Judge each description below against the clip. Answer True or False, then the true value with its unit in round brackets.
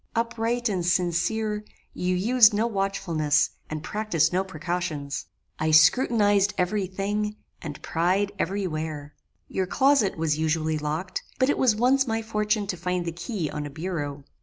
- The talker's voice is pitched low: False (185 Hz)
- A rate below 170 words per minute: True (155 wpm)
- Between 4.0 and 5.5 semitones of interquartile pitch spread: True (5.0 semitones)